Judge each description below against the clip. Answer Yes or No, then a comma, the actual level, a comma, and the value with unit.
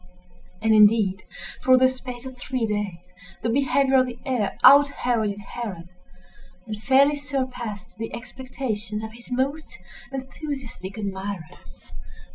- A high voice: Yes, high, 240 Hz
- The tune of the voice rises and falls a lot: No, average, 3.8 semitones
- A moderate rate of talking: No, slow, 125 wpm